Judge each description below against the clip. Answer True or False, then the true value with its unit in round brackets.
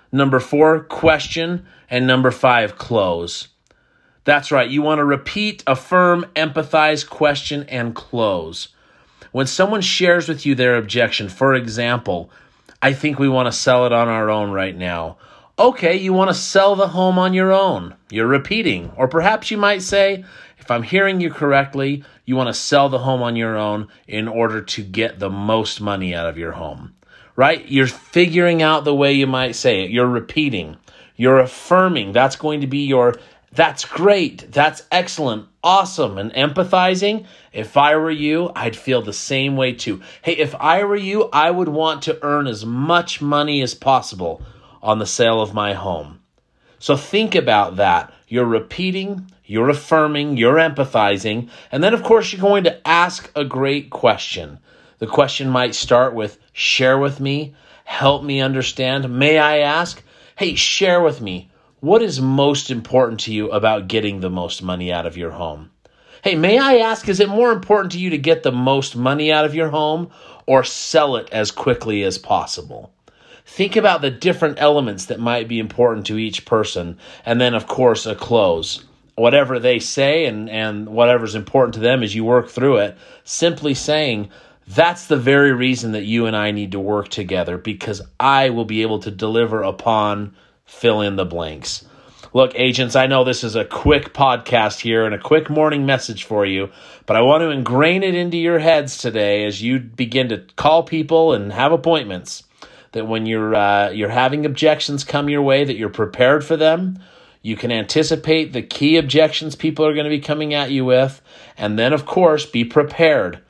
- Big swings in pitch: True (5.8 semitones)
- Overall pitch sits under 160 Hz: True (135 Hz)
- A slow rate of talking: False (185 wpm)